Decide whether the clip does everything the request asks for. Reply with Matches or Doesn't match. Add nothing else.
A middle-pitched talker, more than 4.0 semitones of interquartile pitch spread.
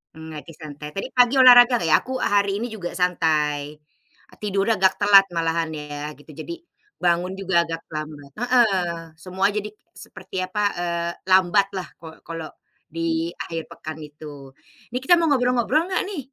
Matches